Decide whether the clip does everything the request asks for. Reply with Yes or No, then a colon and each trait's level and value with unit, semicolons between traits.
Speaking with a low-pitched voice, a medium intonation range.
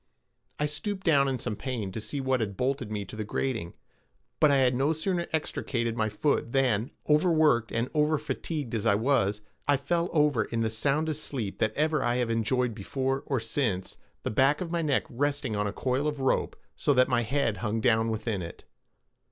Yes: low, 130 Hz; average, 4.6 semitones